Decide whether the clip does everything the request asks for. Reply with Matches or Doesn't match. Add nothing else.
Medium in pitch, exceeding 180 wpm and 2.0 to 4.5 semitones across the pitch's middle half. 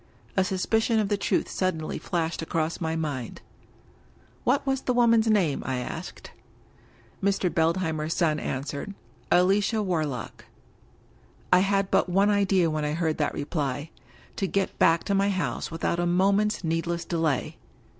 Doesn't match